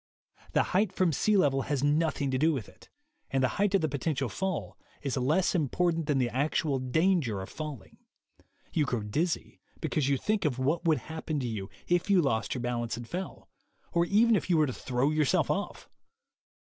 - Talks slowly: No, average, 200 wpm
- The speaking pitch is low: No, medium, 150 Hz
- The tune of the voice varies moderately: Yes, average, 4.8 semitones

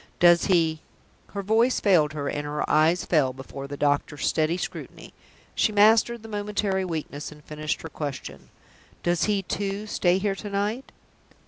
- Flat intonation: No, wide, 5.4 semitones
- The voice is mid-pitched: Yes, medium, 175 Hz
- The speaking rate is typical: Yes, average, 165 wpm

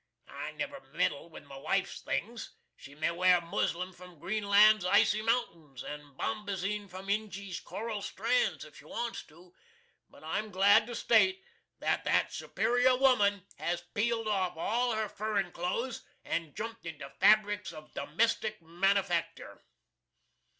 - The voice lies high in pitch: Yes, high, 200 Hz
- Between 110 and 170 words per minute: Yes, average, 140 wpm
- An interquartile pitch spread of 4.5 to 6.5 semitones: No, average, 4.1 semitones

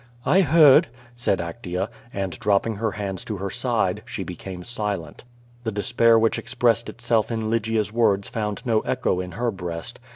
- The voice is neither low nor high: No, low, 110 Hz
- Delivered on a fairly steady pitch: No, average, 3.1 semitones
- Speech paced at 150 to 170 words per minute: Yes, average, 165 wpm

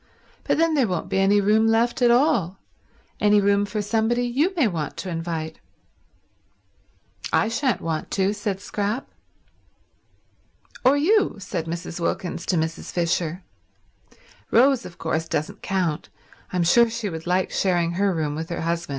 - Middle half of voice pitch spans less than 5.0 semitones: No, average, 5.3 semitones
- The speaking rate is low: No, average, 155 wpm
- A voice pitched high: Yes, high, 195 Hz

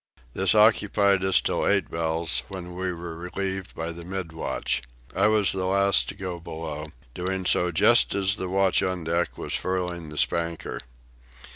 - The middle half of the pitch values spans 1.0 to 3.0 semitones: Yes, narrow, 2.4 semitones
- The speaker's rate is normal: Yes, average, 170 wpm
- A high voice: No, very low, 90 Hz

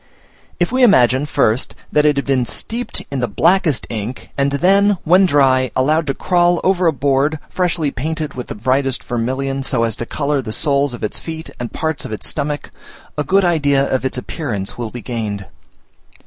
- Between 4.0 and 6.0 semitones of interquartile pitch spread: Yes, average, 4.4 semitones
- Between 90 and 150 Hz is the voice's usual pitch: Yes, medium, 140 Hz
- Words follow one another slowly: No, average, 190 wpm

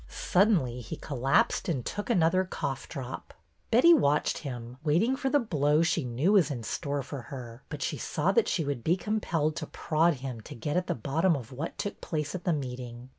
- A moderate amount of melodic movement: No, wide, 5.7 semitones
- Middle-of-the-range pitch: Yes, medium, 150 Hz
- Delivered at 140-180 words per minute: No, fast, 205 wpm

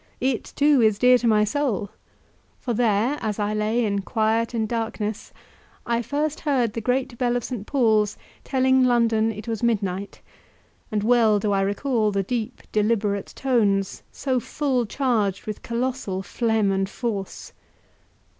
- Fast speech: No, average, 155 wpm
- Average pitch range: Yes, average, 3.1 semitones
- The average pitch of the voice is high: Yes, high, 225 Hz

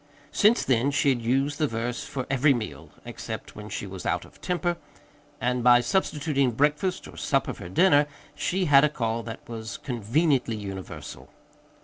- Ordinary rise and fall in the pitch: Yes, average, 4.4 semitones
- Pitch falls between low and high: No, low, 130 Hz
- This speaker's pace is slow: No, average, 165 wpm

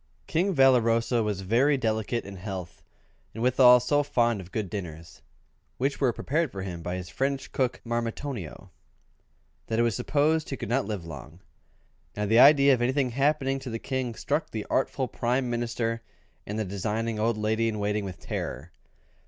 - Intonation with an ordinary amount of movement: Yes, average, 4.2 semitones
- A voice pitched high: No, low, 115 Hz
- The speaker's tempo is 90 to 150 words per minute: No, average, 175 wpm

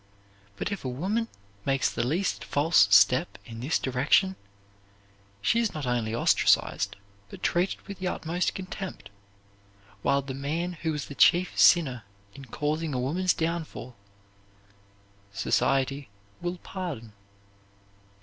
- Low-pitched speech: No, medium, 155 Hz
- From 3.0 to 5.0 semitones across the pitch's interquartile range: No, wide, 5.5 semitones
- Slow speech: Yes, slow, 130 wpm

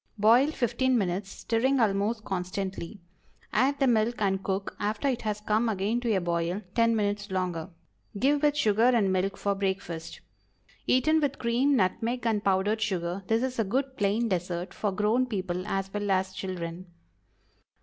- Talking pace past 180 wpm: No, average, 165 wpm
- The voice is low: No, high, 210 Hz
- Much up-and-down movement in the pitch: No, average, 3.8 semitones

